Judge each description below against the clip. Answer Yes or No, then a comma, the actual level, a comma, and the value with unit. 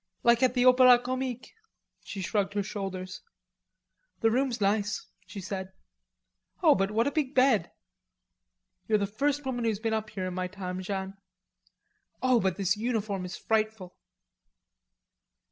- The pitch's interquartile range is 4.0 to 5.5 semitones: Yes, average, 4.3 semitones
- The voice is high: Yes, high, 215 Hz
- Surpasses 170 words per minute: No, average, 145 wpm